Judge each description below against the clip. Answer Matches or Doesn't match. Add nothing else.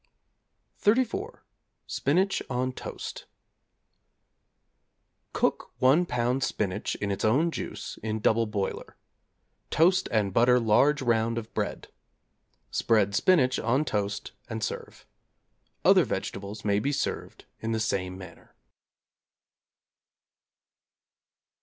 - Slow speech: Matches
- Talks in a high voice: Doesn't match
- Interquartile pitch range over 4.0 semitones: Matches